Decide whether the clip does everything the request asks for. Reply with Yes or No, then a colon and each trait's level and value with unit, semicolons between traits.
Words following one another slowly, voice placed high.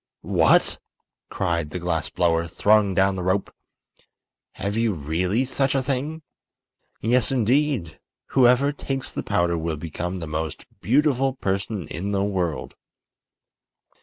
No: slow, 130 wpm; low, 100 Hz